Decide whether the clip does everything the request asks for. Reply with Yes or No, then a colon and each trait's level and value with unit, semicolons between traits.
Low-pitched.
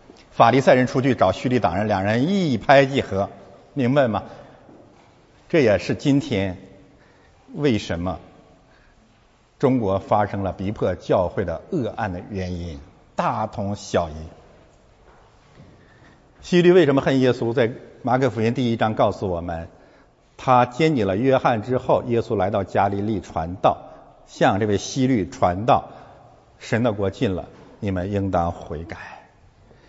Yes: low, 105 Hz